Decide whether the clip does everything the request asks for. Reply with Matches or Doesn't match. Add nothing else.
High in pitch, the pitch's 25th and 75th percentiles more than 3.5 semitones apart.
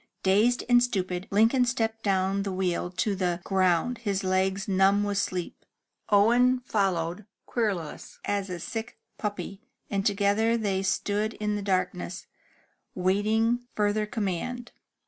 Doesn't match